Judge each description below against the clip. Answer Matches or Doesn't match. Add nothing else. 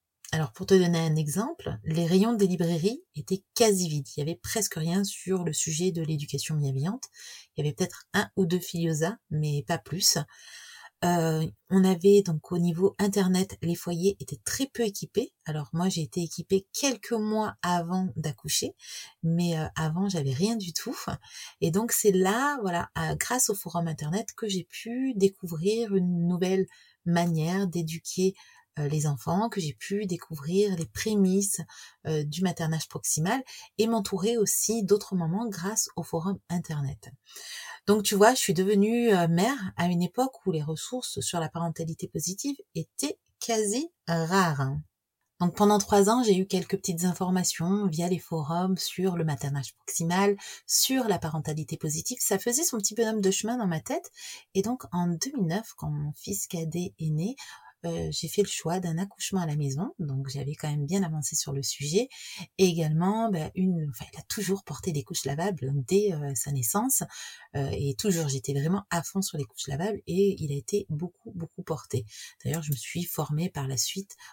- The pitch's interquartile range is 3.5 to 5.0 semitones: Matches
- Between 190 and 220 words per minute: Doesn't match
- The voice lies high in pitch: Doesn't match